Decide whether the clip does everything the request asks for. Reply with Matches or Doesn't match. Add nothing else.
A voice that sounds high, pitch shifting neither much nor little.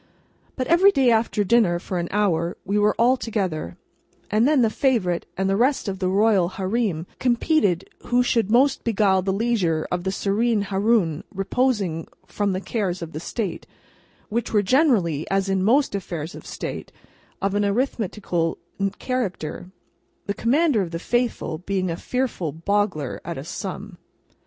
Matches